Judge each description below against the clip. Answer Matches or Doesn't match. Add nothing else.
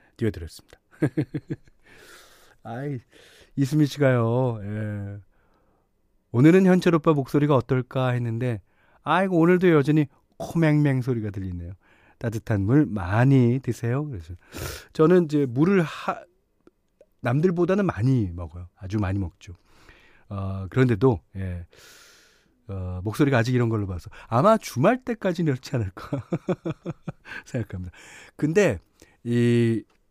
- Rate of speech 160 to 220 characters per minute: Doesn't match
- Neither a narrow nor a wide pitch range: Doesn't match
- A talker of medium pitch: Doesn't match